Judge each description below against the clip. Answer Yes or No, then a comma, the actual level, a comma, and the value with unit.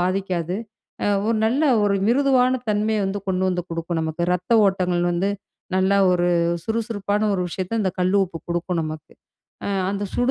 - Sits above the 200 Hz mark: No, high, 190 Hz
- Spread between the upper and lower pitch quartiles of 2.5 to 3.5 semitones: Yes, average, 3.2 semitones